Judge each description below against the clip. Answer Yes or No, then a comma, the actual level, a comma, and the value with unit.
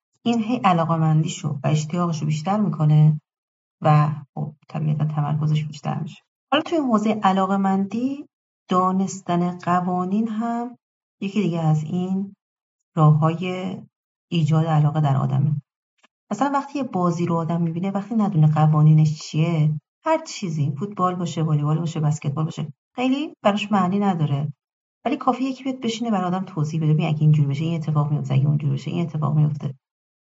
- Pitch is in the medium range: Yes, medium, 170 Hz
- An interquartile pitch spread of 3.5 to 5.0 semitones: Yes, average, 4.5 semitones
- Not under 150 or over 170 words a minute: Yes, fast, 155 wpm